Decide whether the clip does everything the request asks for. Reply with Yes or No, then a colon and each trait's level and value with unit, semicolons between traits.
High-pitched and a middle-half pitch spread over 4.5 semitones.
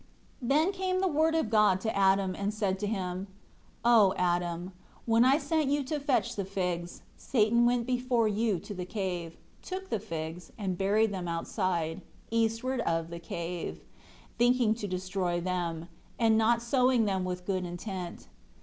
Yes: high, 205 Hz; average, 4.9 semitones